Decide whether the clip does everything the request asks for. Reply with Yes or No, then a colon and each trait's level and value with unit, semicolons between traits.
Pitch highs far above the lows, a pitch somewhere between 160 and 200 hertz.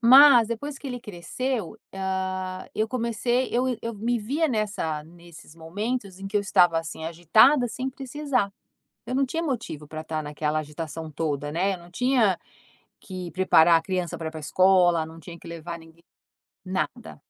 Yes: wide, 6.6 semitones; medium, 185 Hz